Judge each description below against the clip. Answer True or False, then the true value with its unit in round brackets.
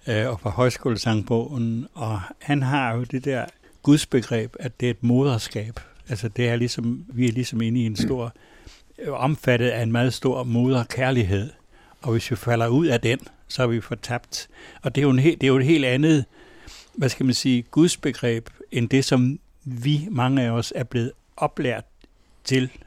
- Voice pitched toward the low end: True (125 Hz)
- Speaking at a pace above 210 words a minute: False (185 wpm)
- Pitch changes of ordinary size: False (2.1 semitones)